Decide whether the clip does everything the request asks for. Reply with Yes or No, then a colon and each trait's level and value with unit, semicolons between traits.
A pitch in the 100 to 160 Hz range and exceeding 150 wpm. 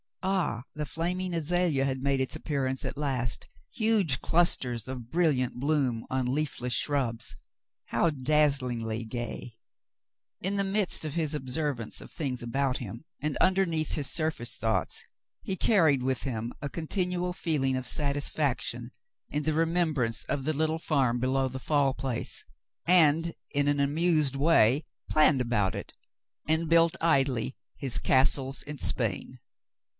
No: medium, 140 Hz; average, 145 wpm